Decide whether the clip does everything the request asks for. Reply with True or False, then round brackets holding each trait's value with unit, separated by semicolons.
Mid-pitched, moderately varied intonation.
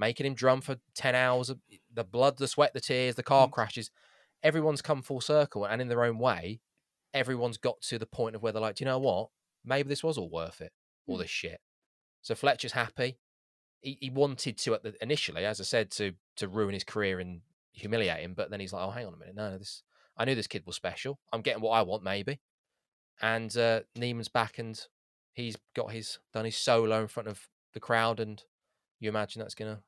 False (115 Hz; 3.5 semitones)